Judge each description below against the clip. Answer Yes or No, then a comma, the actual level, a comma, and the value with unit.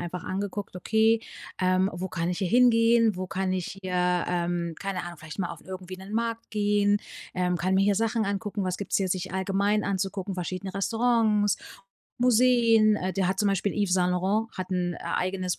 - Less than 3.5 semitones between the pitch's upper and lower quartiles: Yes, narrow, 2.5 semitones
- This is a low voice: No, high, 190 Hz